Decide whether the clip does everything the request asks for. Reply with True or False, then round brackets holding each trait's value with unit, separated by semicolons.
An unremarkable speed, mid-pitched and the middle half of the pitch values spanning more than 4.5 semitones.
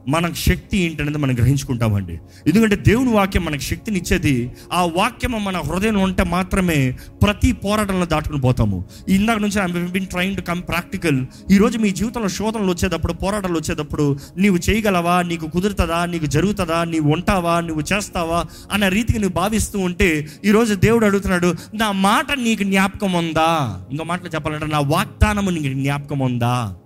False (145 wpm; 175 Hz; 4.9 semitones)